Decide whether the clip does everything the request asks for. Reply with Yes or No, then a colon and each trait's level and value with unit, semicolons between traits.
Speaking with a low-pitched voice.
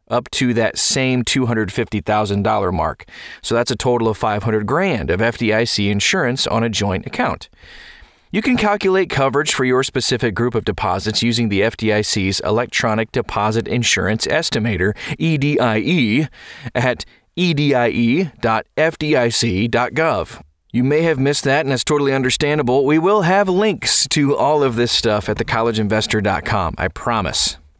Yes: low, 120 Hz